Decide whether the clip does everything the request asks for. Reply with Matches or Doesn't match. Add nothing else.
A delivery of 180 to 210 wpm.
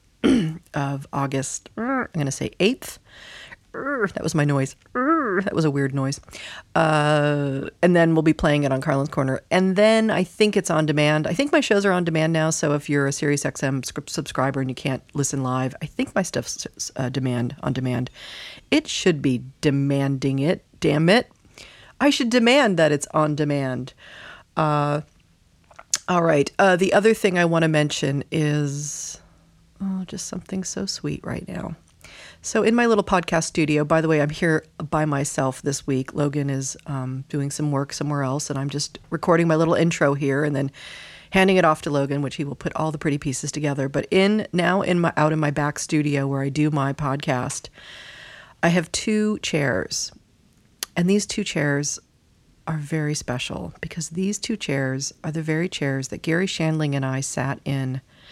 Matches